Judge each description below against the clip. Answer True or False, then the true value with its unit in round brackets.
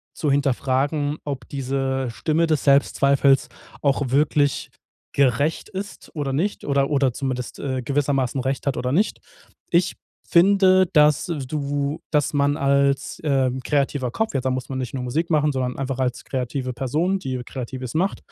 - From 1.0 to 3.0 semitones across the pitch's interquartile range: True (2.4 semitones)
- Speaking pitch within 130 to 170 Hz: True (140 Hz)